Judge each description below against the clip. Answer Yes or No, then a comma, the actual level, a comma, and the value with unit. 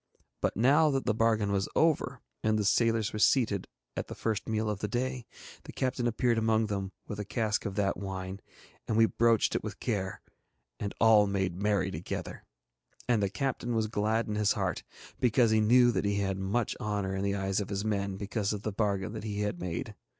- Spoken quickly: Yes, fast, 210 wpm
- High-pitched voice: No, low, 105 Hz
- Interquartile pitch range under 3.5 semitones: Yes, narrow, 2.5 semitones